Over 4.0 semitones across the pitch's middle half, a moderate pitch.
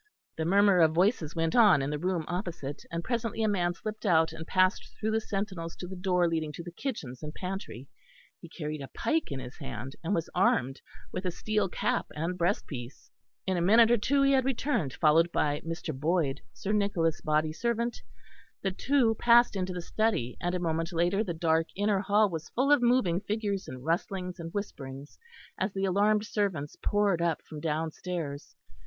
Yes: average, 4.4 semitones; medium, 180 Hz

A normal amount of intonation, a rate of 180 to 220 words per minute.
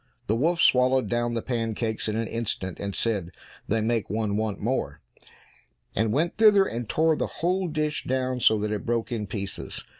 Yes: average, 3.5 semitones; average, 185 wpm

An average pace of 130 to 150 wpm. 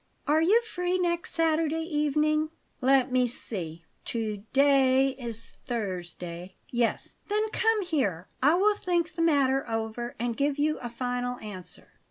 Yes: average, 145 wpm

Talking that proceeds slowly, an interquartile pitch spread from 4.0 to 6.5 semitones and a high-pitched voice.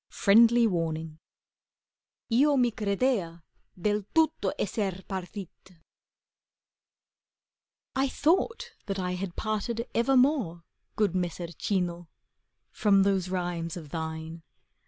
Yes: slow, 95 wpm; average, 5.1 semitones; high, 195 Hz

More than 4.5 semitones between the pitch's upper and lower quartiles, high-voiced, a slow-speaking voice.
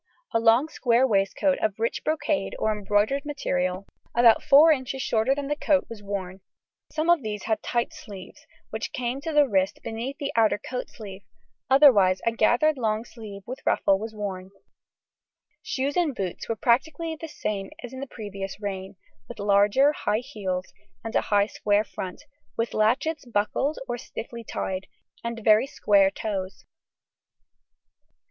No: average, 5.1 semitones; high, 225 Hz; average, 160 wpm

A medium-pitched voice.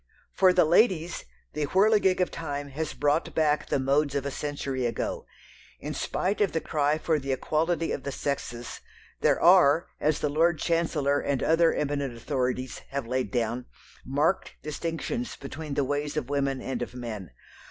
Yes: medium, 145 Hz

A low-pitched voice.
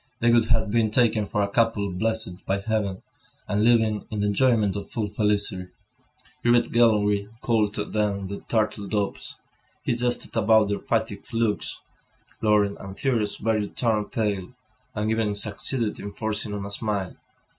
Yes: low, 105 Hz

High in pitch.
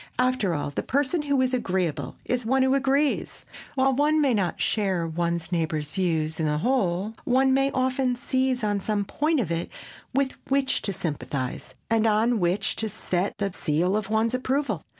Yes: high, 220 Hz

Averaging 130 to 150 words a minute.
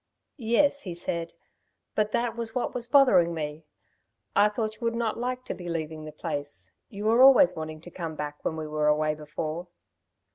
No: average, 190 wpm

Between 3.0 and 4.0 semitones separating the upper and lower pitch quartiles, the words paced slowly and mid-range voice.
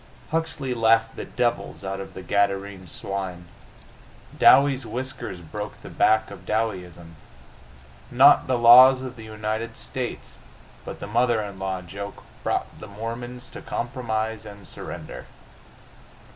No: average, 3.7 semitones; slow, 130 wpm; low, 110 Hz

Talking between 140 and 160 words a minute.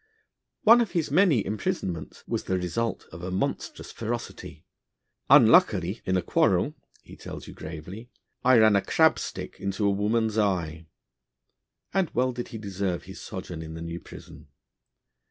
Yes: average, 155 wpm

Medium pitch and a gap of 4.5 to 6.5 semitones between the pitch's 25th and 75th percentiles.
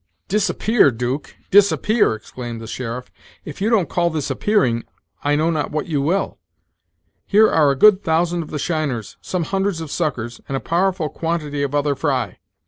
Yes: medium, 155 Hz; average, 5.0 semitones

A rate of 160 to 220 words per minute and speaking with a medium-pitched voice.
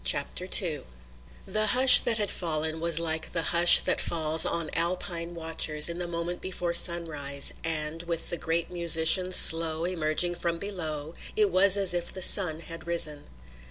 Yes: average, 165 wpm; medium, 170 Hz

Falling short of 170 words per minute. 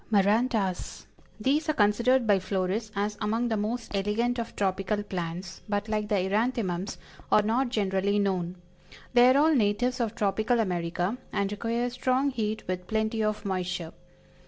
Yes: average, 155 wpm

